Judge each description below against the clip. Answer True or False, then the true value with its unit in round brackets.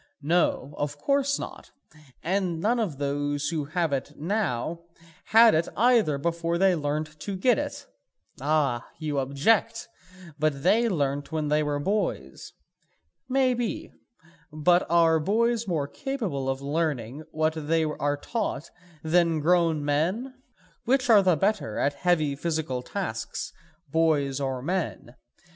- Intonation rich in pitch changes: False (4.9 semitones)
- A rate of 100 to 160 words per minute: True (135 wpm)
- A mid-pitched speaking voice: True (160 Hz)